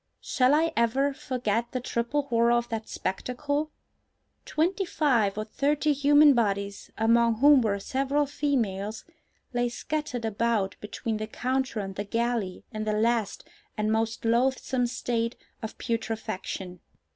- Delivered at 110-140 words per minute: Yes, slow, 135 wpm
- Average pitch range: Yes, average, 3.9 semitones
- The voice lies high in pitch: Yes, high, 235 Hz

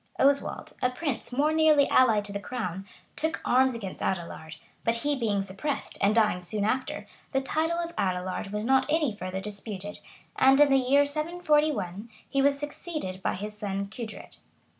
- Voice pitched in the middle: No, high, 240 Hz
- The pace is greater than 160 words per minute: Yes, average, 170 wpm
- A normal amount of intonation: No, wide, 6.1 semitones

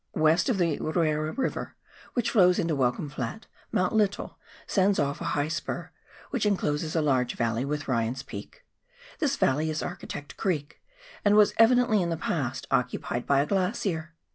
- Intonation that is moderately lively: No, wide, 5.8 semitones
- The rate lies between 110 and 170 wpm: Yes, average, 165 wpm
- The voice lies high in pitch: No, medium, 160 Hz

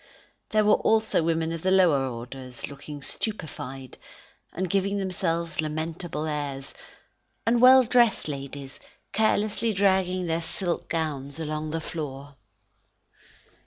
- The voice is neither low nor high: Yes, medium, 165 Hz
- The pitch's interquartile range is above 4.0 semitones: Yes, average, 5.2 semitones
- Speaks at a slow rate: Yes, slow, 120 wpm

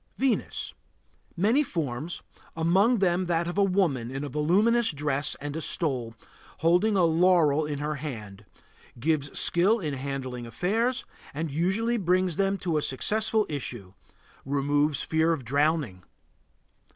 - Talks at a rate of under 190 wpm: Yes, average, 140 wpm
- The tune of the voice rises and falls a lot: No, average, 5.0 semitones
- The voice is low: No, medium, 160 Hz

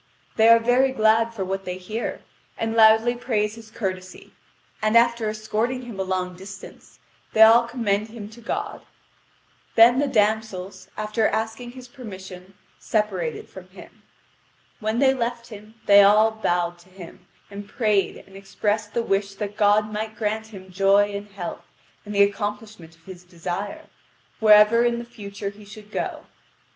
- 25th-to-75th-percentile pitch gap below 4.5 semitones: Yes, narrow, 2.5 semitones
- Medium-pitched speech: No, high, 210 Hz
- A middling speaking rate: Yes, average, 160 wpm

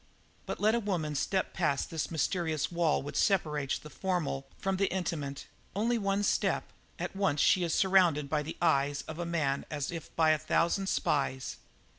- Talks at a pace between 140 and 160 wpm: No, average, 180 wpm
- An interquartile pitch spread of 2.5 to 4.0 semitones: No, average, 4.4 semitones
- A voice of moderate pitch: Yes, medium, 165 Hz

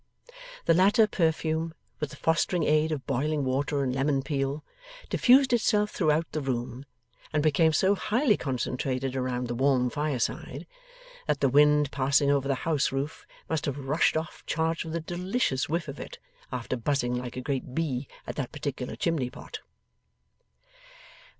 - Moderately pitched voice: Yes, medium, 145 Hz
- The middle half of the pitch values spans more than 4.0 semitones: No, average, 3.5 semitones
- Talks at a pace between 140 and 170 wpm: Yes, average, 155 wpm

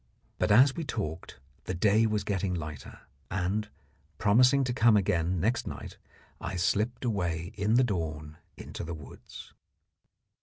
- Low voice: Yes, low, 100 Hz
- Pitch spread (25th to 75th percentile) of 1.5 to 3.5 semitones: No, average, 4.7 semitones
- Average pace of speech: Yes, average, 145 wpm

